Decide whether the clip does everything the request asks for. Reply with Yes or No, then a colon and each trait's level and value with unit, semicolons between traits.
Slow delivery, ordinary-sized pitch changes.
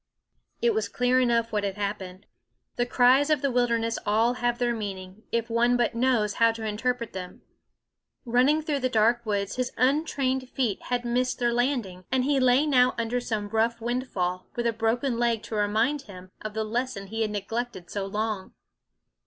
No: average, 185 wpm; average, 3.0 semitones